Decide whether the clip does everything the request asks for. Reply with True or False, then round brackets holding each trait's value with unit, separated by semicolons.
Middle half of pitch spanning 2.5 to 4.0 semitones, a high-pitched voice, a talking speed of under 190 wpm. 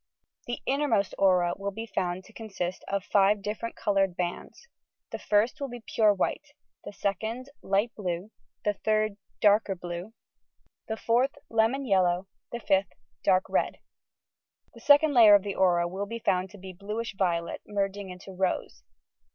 True (3.0 semitones; 200 Hz; 160 wpm)